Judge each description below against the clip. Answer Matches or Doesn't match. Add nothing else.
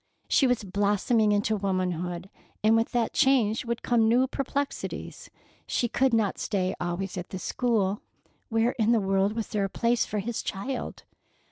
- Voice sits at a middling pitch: Doesn't match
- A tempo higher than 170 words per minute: Doesn't match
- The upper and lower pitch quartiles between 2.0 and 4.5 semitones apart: Matches